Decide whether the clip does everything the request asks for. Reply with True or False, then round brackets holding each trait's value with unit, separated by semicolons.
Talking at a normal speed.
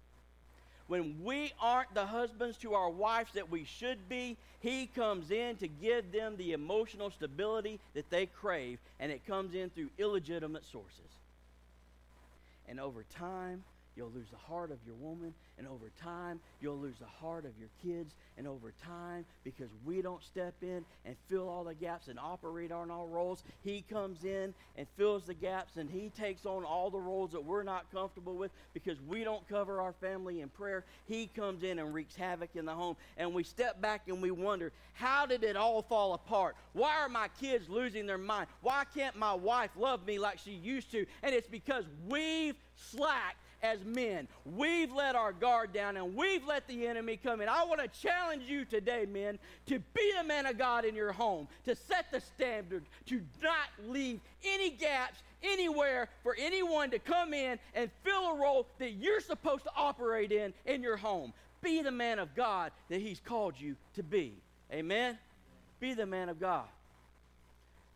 True (190 wpm)